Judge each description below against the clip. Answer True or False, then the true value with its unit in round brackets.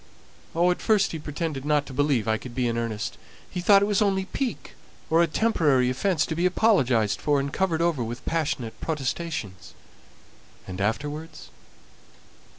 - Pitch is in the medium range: True (150 Hz)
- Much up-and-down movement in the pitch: True (5.9 semitones)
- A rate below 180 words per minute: True (165 wpm)